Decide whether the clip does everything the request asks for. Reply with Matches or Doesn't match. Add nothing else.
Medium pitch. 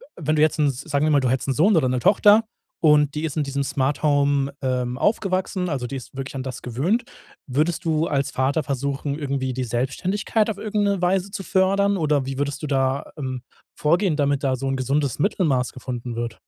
Matches